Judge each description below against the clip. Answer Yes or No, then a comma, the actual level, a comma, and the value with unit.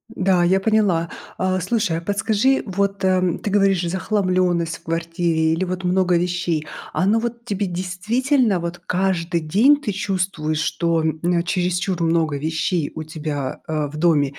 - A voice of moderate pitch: Yes, medium, 180 Hz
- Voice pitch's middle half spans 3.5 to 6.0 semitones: No, average, 2.9 semitones